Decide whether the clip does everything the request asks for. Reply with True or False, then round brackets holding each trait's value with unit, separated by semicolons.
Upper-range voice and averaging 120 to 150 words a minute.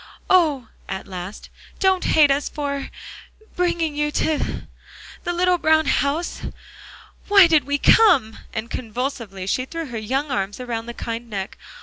True (280 Hz; 145 wpm)